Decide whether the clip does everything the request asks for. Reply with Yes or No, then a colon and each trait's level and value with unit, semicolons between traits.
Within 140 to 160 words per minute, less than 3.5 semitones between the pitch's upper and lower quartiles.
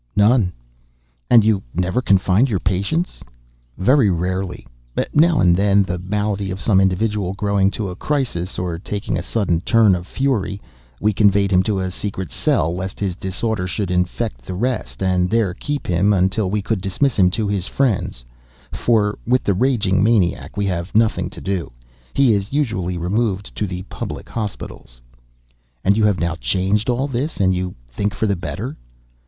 No: average, 170 wpm; average, 3.1 semitones